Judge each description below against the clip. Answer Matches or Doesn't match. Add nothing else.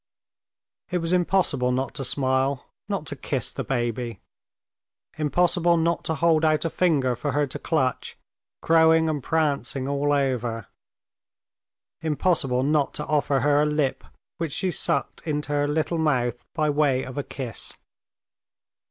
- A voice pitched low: Doesn't match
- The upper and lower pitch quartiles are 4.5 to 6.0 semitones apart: Doesn't match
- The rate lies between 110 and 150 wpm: Matches